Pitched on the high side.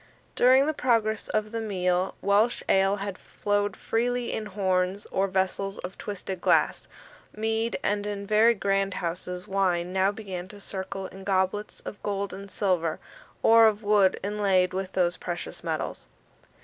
Yes: high, 195 Hz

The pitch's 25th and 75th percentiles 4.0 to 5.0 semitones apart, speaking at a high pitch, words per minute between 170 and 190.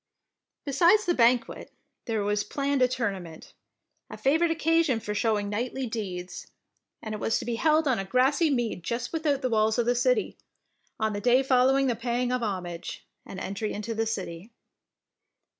Yes: average, 4.4 semitones; high, 240 Hz; average, 175 wpm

